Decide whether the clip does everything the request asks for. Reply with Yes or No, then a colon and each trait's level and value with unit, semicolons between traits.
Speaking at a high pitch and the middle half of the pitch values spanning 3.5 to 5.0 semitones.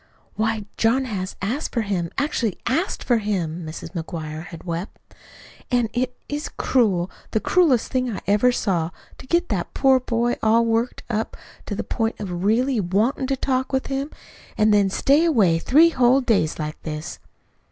No: high, 225 Hz; wide, 5.5 semitones